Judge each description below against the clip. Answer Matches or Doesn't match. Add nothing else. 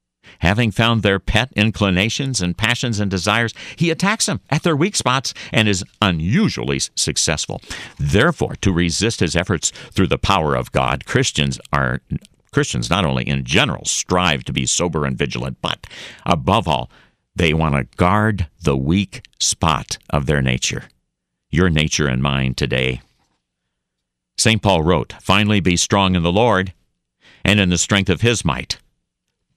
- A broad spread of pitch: Matches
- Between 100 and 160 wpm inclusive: Matches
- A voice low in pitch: Matches